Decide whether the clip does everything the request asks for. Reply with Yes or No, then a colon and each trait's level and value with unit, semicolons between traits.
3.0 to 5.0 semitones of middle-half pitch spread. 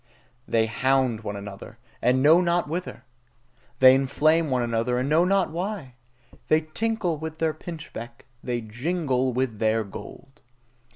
No: wide, 5.5 semitones